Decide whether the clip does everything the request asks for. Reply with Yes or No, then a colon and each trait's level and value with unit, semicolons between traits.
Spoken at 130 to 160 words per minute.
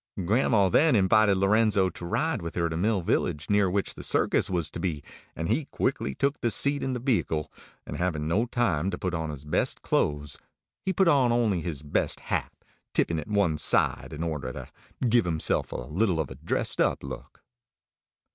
No: average, 195 wpm